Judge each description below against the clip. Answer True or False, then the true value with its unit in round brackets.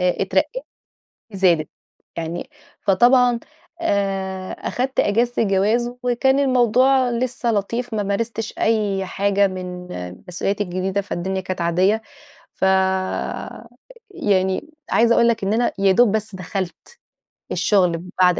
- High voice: True (200 Hz)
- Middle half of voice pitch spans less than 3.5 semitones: False (4.1 semitones)